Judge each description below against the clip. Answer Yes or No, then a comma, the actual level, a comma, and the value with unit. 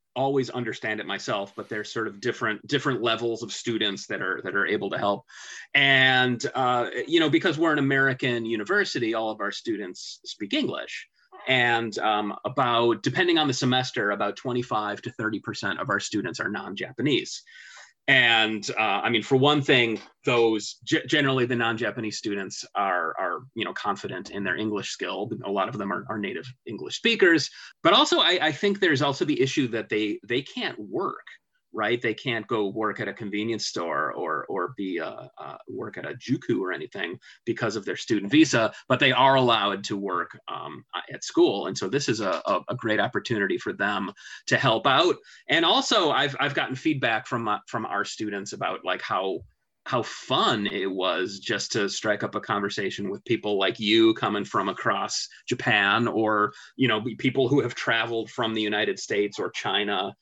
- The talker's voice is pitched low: Yes, low, 115 Hz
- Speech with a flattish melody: No, average, 4.1 semitones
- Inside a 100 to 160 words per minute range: No, average, 185 wpm